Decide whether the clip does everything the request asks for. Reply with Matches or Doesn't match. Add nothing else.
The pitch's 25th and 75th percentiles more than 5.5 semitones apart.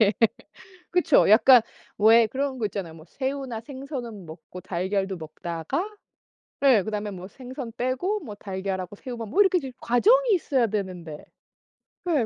Matches